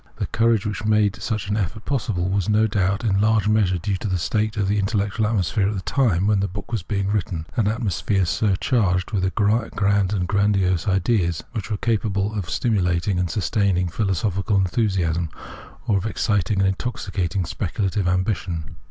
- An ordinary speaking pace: Yes, average, 175 wpm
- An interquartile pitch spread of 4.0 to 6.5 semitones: No, narrow, 2.5 semitones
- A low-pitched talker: Yes, low, 100 Hz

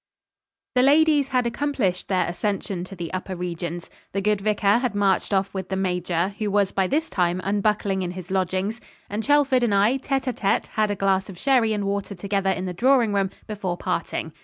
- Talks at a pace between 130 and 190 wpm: No, fast, 205 wpm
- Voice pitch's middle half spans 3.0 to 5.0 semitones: Yes, average, 3.3 semitones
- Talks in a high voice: Yes, high, 200 Hz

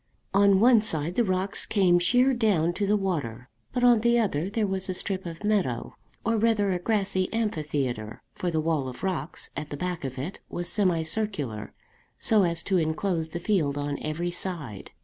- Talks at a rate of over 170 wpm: Yes, average, 190 wpm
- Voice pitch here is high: No, medium, 180 Hz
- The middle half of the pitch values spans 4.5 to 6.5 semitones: Yes, average, 4.9 semitones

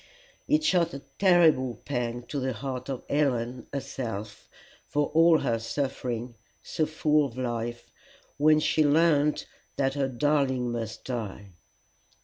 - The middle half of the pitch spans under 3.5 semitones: No, average, 4.0 semitones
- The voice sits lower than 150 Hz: Yes, low, 135 Hz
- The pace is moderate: No, slow, 130 wpm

